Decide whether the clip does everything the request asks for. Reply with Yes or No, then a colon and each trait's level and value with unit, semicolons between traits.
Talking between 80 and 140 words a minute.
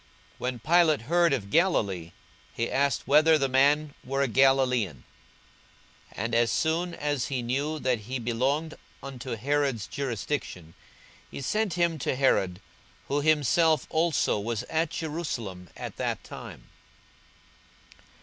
Yes: slow, 135 wpm